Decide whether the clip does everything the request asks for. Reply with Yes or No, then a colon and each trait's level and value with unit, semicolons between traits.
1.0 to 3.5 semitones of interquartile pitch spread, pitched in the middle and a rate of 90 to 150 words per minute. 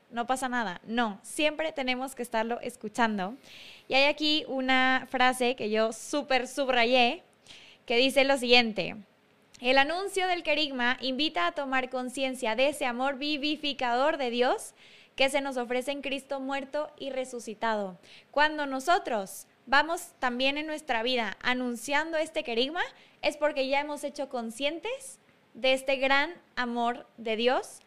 No: average, 3.2 semitones; very high, 265 Hz; average, 145 wpm